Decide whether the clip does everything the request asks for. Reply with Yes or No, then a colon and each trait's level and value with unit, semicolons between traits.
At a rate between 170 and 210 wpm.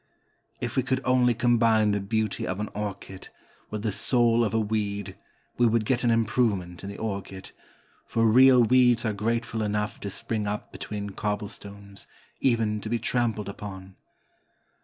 No: average, 160 wpm